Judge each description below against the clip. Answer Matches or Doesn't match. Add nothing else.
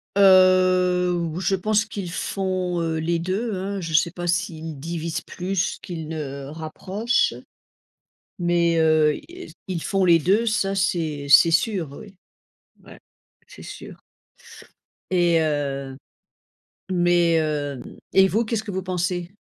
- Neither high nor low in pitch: Matches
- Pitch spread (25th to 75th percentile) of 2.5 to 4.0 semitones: Matches